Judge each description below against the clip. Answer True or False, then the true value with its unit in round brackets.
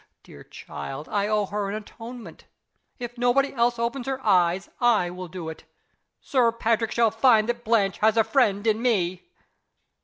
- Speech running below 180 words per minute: True (165 wpm)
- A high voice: True (225 Hz)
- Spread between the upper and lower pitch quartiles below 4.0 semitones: True (3.3 semitones)